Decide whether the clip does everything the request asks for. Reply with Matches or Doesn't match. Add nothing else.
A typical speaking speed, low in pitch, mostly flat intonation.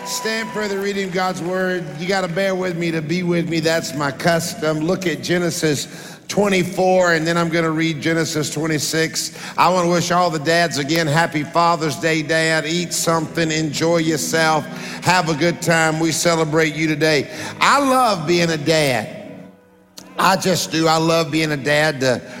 Doesn't match